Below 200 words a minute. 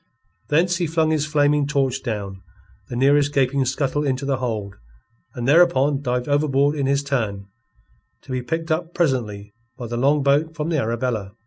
Yes: average, 170 wpm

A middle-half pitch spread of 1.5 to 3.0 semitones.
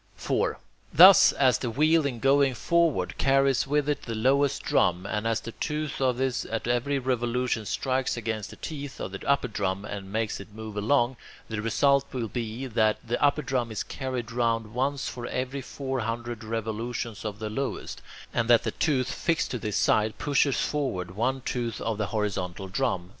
No: average, 3.7 semitones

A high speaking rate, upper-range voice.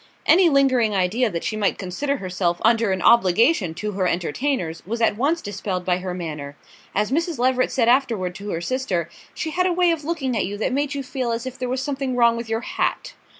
Yes: fast, 225 wpm; high, 230 Hz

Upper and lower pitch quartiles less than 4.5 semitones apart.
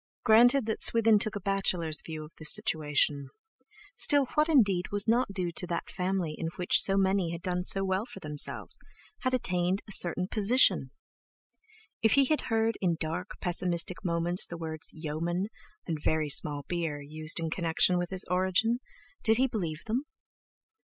No: average, 4.8 semitones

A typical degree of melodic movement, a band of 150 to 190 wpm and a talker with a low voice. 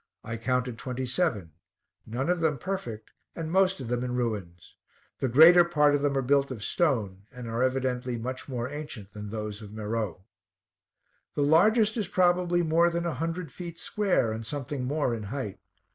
No: wide, 6.4 semitones; average, 180 wpm; low, 130 Hz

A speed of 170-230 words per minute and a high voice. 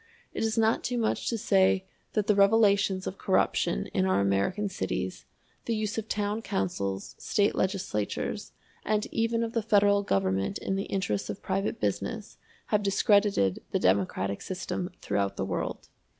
No: average, 160 wpm; high, 195 Hz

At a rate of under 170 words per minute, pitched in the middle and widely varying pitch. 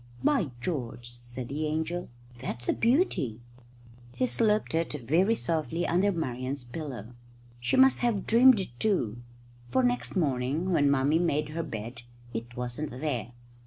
Yes: average, 145 wpm; medium, 150 Hz; wide, 7.0 semitones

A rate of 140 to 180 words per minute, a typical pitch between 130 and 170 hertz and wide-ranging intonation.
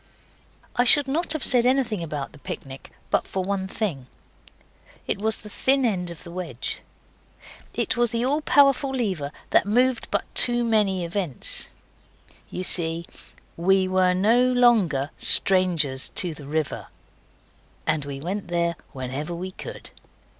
No: average, 145 wpm; medium, 185 Hz; wide, 6.7 semitones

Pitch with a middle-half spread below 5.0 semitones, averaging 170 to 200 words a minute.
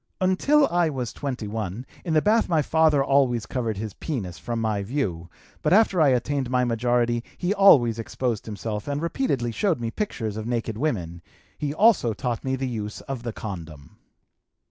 No: wide, 5.5 semitones; average, 175 wpm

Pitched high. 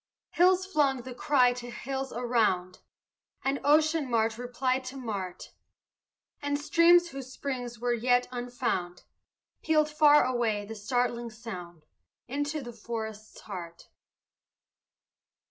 Yes: high, 245 Hz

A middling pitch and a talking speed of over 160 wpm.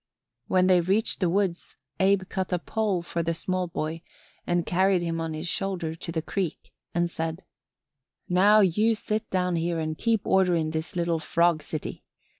Yes: medium, 175 Hz; average, 180 wpm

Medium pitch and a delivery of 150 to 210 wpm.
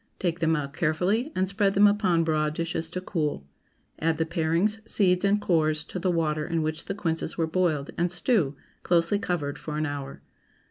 Yes: medium, 165 Hz; average, 190 wpm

